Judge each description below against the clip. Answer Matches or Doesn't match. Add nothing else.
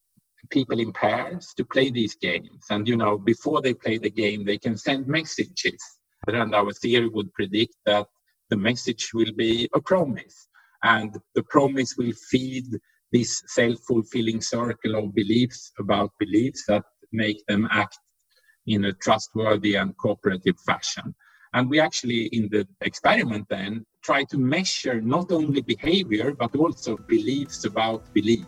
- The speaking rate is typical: Matches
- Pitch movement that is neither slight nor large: Matches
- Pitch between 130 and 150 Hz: Doesn't match